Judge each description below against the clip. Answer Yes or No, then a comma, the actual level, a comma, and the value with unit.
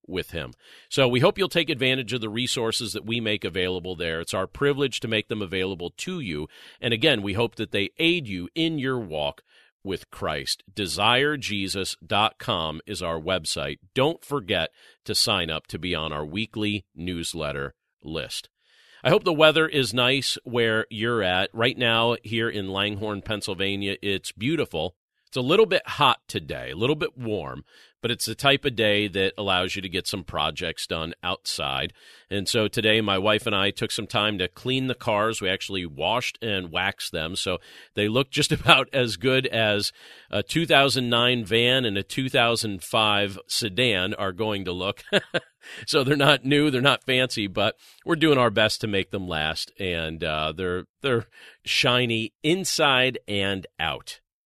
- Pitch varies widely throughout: No, average, 4.8 semitones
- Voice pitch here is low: Yes, low, 110 Hz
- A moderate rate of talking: Yes, average, 175 wpm